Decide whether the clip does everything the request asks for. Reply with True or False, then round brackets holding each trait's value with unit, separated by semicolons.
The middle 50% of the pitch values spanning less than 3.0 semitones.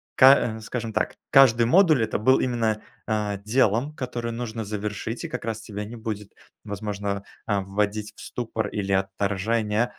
True (2.5 semitones)